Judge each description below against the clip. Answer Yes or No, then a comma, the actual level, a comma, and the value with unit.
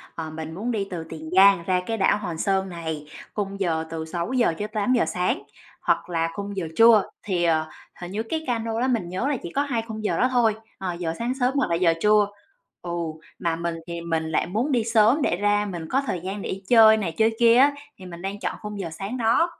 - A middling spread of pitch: Yes, average, 4.9 semitones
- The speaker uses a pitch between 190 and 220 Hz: Yes, high, 195 Hz